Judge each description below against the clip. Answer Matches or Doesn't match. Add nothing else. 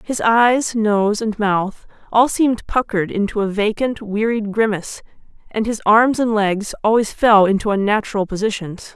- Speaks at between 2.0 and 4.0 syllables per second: Doesn't match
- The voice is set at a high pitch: Matches